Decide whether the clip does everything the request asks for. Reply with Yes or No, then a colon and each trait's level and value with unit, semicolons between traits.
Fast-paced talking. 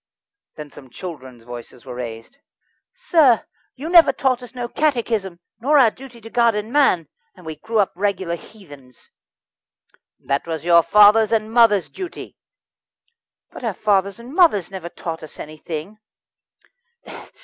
No: average, 150 wpm